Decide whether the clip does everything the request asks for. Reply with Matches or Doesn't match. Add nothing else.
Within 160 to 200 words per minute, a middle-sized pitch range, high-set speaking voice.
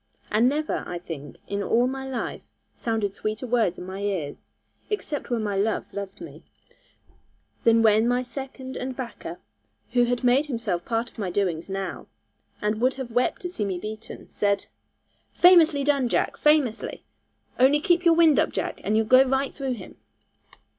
Matches